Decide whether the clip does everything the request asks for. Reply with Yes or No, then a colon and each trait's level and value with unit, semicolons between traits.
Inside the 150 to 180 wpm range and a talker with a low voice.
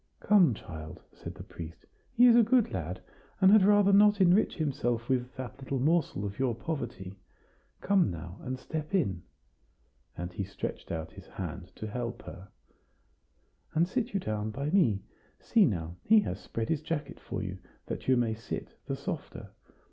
Yes: average, 175 wpm; low, 130 Hz